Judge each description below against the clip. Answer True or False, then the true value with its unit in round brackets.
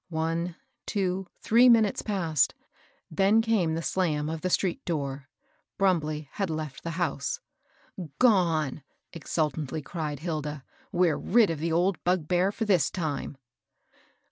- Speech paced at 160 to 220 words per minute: False (135 wpm)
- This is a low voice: False (165 Hz)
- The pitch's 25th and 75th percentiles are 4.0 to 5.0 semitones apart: False (3.6 semitones)